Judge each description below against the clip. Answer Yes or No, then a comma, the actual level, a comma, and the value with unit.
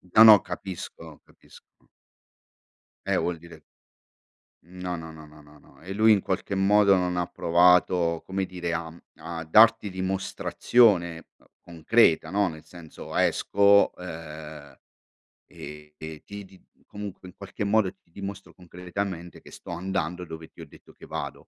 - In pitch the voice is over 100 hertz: No, very low, 90 Hz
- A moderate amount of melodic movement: Yes, average, 3.2 semitones